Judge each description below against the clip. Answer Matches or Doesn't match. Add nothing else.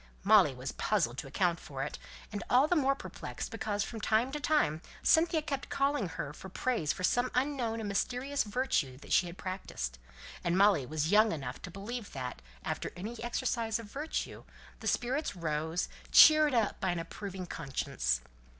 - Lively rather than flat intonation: Matches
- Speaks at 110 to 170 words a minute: Doesn't match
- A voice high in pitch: Matches